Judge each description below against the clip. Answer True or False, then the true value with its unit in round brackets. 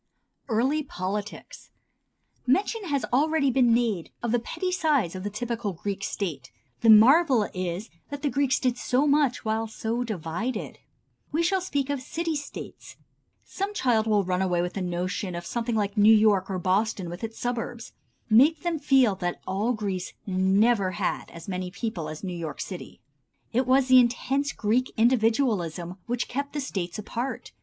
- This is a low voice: False (225 Hz)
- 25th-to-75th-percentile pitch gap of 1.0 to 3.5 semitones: False (5.6 semitones)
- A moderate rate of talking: True (170 wpm)